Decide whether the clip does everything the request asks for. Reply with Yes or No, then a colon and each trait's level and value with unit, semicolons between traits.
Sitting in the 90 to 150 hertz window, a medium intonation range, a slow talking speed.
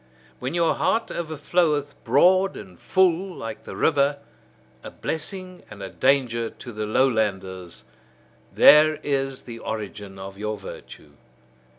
No: low, 135 Hz; wide, 7.1 semitones; slow, 125 wpm